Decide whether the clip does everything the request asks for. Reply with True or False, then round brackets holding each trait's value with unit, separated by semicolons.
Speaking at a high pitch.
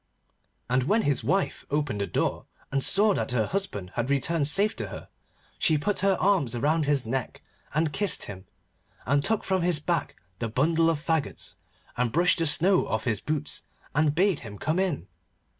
False (150 Hz)